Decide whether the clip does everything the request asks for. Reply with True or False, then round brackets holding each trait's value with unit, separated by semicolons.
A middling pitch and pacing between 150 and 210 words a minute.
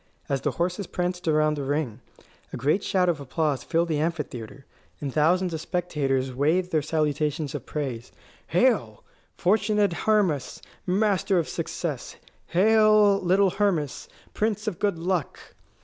False (165 Hz; 140 wpm)